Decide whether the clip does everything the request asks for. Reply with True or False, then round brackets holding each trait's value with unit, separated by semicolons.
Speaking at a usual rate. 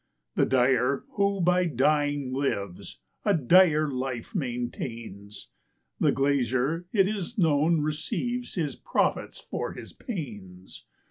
False (115 wpm)